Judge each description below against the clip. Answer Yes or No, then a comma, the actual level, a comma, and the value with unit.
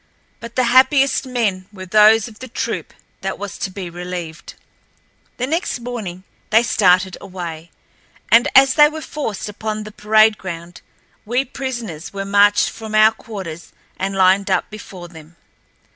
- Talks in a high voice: Yes, high, 210 Hz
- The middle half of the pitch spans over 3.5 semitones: Yes, average, 4.1 semitones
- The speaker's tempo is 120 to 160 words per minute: Yes, average, 155 wpm